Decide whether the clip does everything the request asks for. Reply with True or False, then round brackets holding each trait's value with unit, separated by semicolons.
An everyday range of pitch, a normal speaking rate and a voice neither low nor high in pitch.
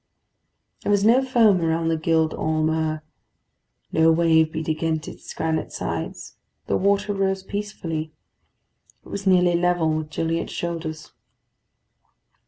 False (3.3 semitones; 130 wpm; 165 Hz)